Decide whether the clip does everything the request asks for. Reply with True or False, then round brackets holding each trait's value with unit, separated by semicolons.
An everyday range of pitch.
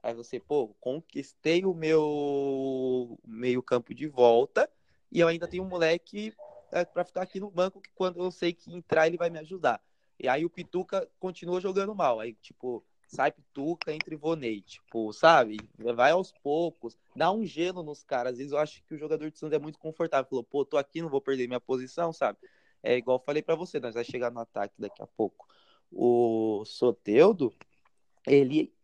False (5.7 semitones)